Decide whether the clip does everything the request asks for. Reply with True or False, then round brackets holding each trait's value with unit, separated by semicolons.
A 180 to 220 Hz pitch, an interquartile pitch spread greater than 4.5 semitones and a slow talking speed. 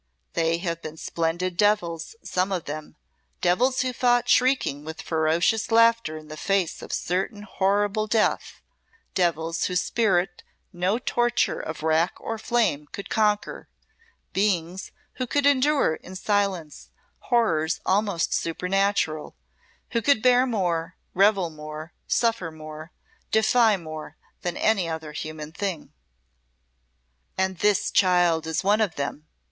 True (185 Hz; 5.0 semitones; 130 wpm)